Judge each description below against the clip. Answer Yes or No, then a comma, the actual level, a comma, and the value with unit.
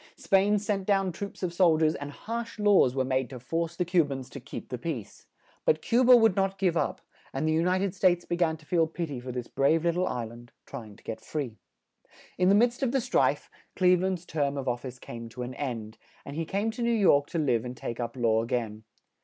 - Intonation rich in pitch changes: Yes, wide, 7.1 semitones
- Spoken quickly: Yes, fast, 255 wpm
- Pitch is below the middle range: No, medium, 160 Hz